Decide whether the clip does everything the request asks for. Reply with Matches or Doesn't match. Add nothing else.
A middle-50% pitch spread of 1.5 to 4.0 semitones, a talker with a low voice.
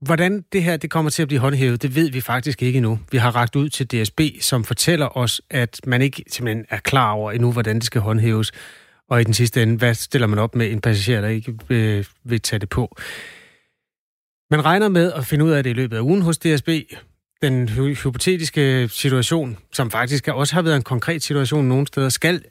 Doesn't match